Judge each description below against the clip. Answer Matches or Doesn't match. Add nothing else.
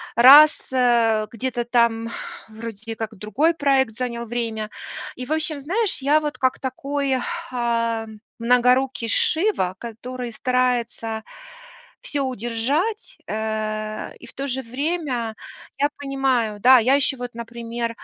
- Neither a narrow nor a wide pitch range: Matches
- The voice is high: Matches